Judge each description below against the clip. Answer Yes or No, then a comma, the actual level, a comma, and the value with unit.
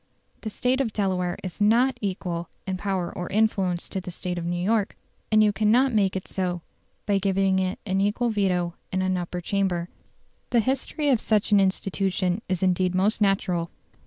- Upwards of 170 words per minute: Yes, average, 185 wpm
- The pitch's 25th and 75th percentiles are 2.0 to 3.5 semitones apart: Yes, average, 2.7 semitones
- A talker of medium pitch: No, high, 195 Hz